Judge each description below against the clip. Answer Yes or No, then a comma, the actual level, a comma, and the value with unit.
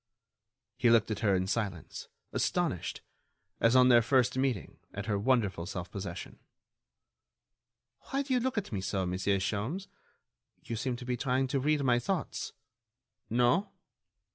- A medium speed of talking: Yes, average, 150 wpm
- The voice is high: No, low, 120 Hz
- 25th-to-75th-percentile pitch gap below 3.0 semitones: No, average, 4.9 semitones